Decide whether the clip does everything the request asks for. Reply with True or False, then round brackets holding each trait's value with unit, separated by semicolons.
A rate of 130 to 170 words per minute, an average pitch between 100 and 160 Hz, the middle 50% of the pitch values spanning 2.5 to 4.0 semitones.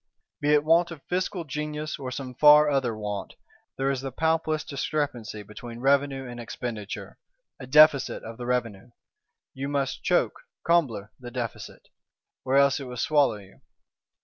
True (155 wpm; 135 Hz; 3.7 semitones)